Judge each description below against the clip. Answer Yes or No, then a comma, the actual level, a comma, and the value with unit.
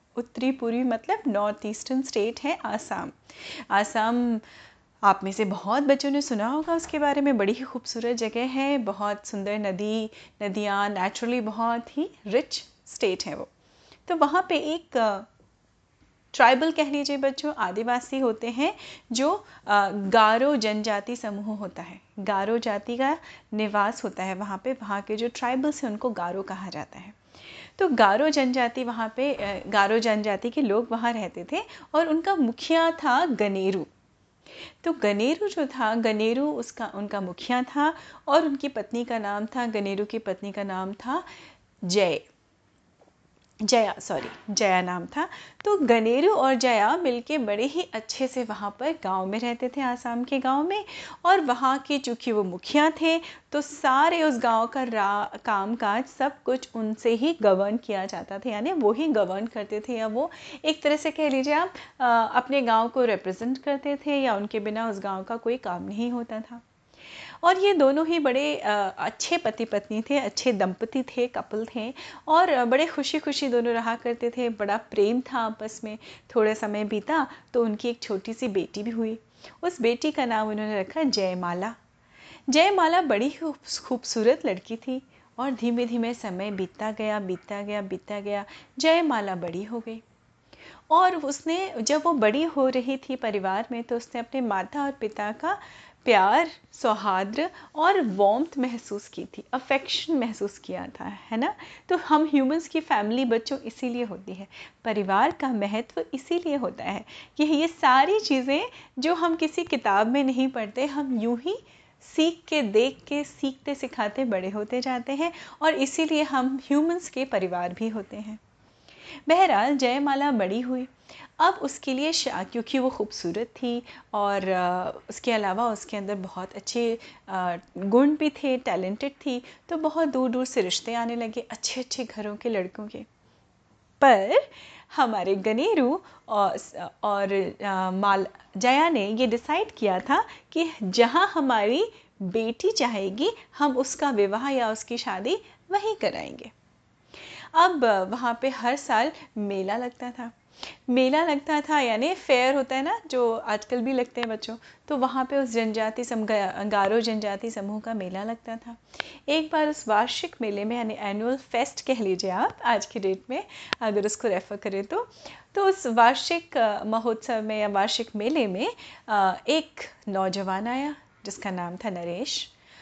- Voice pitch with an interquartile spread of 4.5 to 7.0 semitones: Yes, average, 5.3 semitones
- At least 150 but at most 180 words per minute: Yes, average, 160 wpm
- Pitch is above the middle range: Yes, high, 240 Hz